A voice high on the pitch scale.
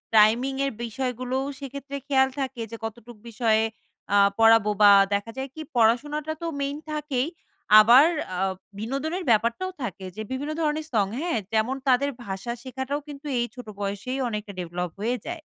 Yes: very high, 250 Hz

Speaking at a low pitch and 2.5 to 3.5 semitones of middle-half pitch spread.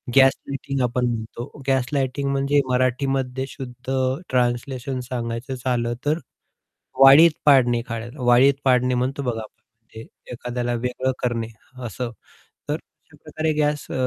No: low, 125 Hz; narrow, 2.1 semitones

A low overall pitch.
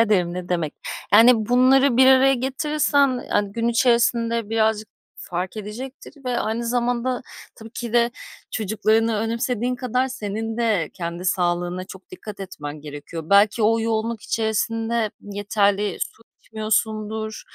No: high, 225 Hz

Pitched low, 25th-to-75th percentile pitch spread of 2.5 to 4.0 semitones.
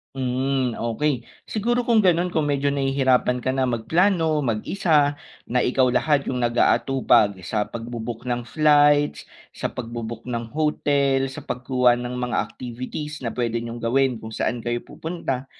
Yes: low, 130 Hz; average, 3.5 semitones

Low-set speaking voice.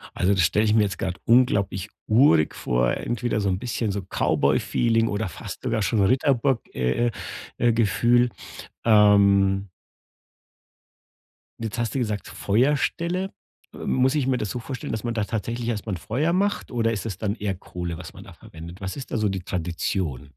Yes: low, 110 Hz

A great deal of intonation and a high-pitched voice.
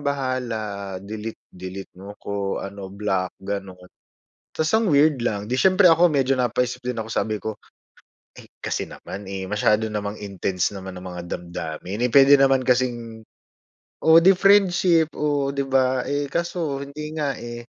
No: wide, 6.0 semitones; low, 120 Hz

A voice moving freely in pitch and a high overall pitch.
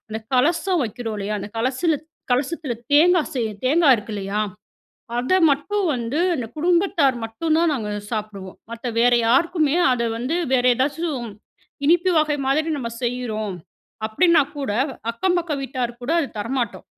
Yes: wide, 6.0 semitones; very high, 260 Hz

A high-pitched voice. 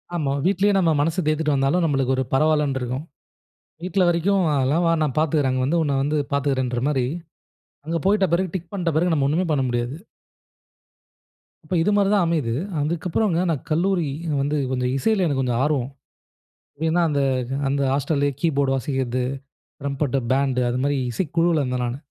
No: medium, 150 Hz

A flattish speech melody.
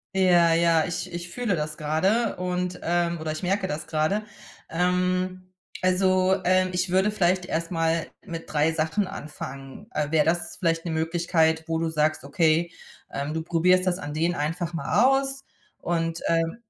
Yes: narrow, 2.3 semitones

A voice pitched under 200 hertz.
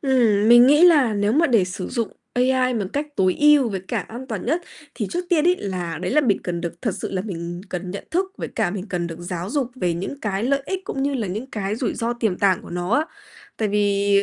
No: high, 215 Hz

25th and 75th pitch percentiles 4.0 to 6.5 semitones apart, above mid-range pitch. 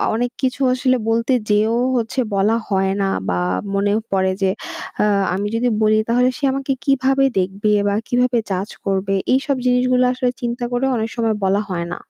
Yes: average, 4.3 semitones; high, 230 Hz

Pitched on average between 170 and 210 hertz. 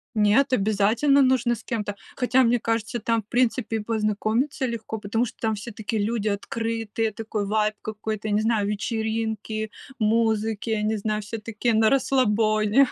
No: high, 220 Hz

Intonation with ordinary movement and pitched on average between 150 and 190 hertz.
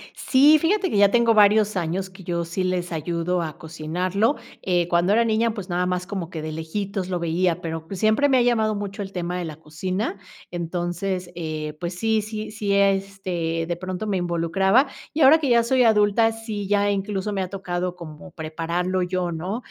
Yes: average, 3.4 semitones; medium, 185 Hz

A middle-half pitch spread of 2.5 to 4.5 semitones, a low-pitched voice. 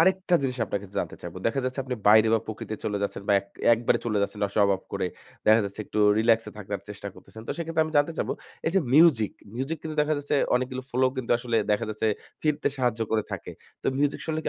No: wide, 5.4 semitones; low, 125 Hz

